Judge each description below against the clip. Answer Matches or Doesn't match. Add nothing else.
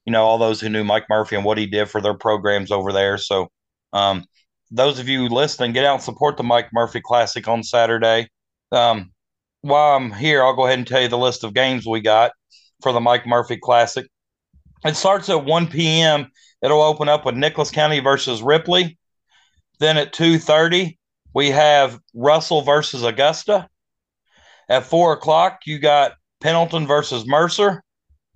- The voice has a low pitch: Matches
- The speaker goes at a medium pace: Matches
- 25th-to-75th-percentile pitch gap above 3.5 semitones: Matches